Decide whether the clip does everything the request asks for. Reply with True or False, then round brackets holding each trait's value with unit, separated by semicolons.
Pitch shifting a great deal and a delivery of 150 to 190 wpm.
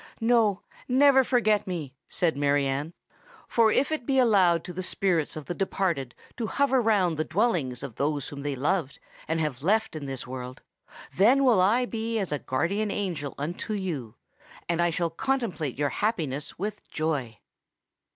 True (7.2 semitones; 165 wpm)